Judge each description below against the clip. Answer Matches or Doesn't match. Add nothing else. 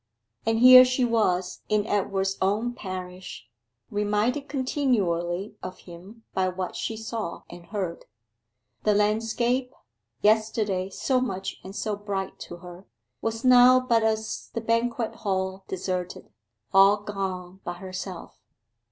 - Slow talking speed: Matches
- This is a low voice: Doesn't match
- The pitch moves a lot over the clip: Doesn't match